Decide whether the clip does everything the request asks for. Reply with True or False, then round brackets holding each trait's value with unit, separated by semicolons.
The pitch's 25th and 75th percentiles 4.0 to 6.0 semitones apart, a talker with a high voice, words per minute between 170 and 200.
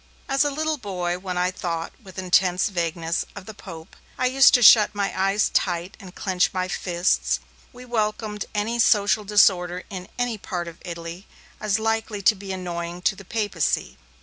False (3.1 semitones; 195 Hz; 175 wpm)